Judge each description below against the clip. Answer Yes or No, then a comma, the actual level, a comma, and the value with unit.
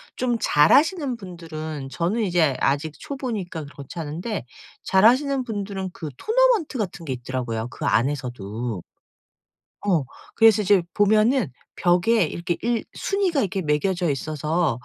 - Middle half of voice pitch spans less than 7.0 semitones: No, wide, 7.4 semitones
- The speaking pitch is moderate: Yes, medium, 180 Hz